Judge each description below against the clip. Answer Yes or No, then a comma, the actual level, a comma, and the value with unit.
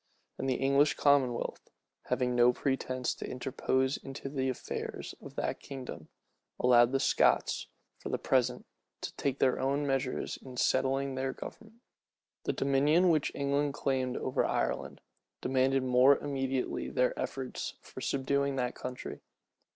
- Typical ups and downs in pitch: No, narrow, 1.5 semitones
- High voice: No, low, 135 Hz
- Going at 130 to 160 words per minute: Yes, average, 140 wpm